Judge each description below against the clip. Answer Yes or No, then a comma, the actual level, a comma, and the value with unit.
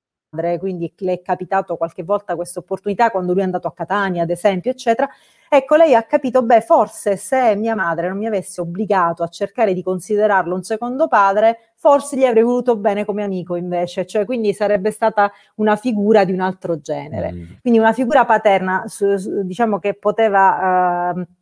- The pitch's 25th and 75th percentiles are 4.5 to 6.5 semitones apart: No, average, 3.8 semitones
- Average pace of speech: No, fast, 180 wpm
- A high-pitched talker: Yes, high, 200 Hz